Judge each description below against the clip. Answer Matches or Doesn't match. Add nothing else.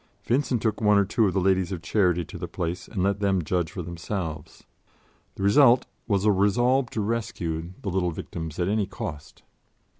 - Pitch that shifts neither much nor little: Matches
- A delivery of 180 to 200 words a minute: Matches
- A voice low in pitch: Matches